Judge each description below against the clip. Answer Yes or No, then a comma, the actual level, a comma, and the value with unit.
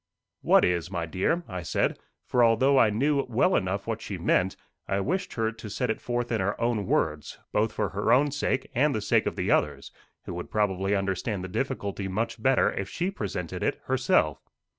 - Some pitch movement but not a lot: Yes, average, 4.5 semitones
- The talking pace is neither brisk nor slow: No, fast, 210 wpm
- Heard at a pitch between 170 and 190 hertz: No, low, 105 Hz